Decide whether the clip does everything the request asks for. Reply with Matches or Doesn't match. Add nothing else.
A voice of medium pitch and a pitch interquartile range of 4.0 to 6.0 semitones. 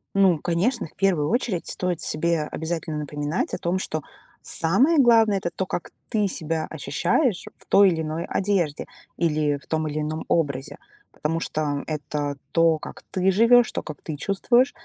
Matches